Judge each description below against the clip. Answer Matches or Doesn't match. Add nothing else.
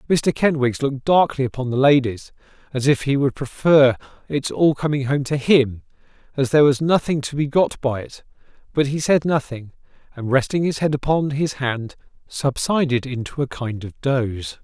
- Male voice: Matches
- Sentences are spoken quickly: Doesn't match